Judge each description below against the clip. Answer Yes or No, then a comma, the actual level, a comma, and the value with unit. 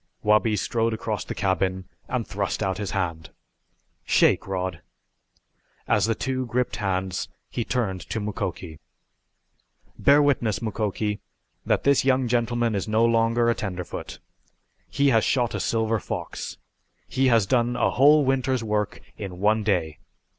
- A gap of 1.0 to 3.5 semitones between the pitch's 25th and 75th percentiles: No, average, 3.9 semitones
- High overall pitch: No, low, 110 Hz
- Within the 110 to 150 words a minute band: Yes, average, 145 wpm